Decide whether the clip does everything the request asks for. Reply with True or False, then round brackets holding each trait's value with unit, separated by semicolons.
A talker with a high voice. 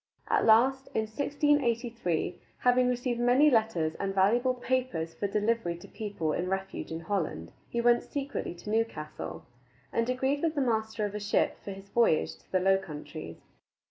True (220 Hz)